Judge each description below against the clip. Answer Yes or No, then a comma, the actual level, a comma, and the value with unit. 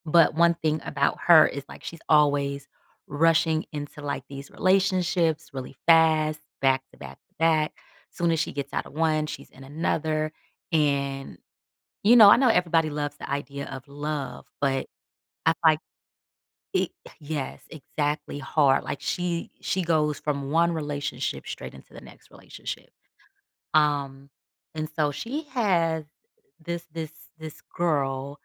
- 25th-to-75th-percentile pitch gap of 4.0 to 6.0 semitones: No, average, 2.7 semitones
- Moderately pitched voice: Yes, medium, 155 Hz